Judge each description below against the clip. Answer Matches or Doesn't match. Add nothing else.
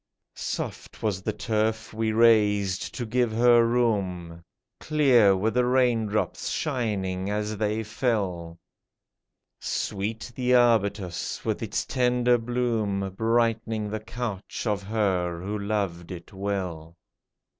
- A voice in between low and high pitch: Doesn't match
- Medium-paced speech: Doesn't match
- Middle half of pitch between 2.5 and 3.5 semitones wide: Matches